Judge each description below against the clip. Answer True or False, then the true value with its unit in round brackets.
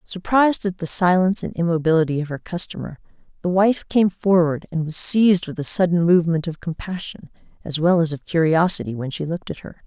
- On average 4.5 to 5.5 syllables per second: False (5.9 syllables/s)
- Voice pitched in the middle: True (170 Hz)